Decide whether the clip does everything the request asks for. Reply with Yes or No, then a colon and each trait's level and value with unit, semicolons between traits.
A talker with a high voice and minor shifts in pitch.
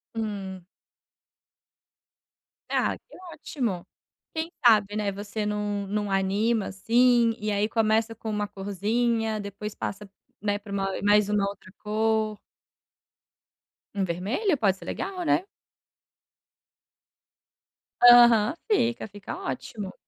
Yes: high, 210 Hz; narrow, 2.1 semitones